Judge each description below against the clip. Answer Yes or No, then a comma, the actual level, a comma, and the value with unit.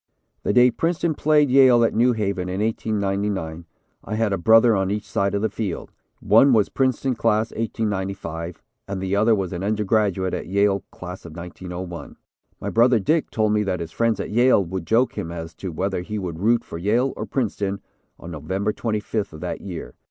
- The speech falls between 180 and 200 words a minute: Yes, average, 195 wpm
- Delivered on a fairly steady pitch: No, average, 3.4 semitones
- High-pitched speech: No, low, 100 Hz